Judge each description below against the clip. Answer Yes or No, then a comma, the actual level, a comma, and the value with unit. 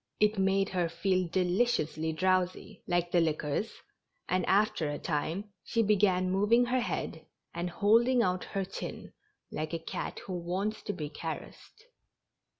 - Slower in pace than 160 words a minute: Yes, average, 150 wpm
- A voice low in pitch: No, medium, 185 Hz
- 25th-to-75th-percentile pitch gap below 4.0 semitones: Yes, average, 3.6 semitones